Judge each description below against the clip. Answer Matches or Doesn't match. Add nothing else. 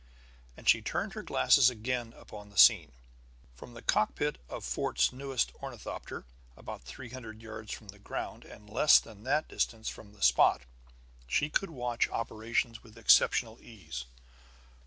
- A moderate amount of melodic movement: Matches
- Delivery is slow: Doesn't match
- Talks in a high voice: Doesn't match